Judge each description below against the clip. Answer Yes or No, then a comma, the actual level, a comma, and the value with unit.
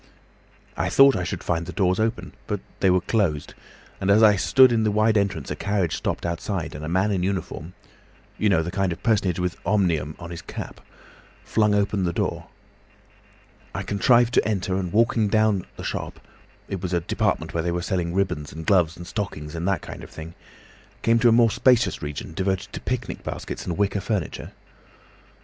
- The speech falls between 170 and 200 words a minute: Yes, average, 190 wpm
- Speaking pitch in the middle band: No, very low, 95 Hz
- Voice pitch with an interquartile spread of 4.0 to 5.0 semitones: No, average, 3.6 semitones